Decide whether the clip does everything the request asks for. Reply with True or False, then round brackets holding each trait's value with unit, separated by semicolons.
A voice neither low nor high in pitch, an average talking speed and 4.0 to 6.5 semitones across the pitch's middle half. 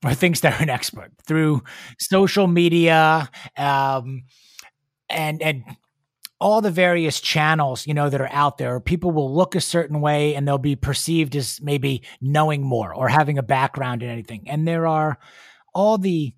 False (150 Hz; 170 wpm; 3.0 semitones)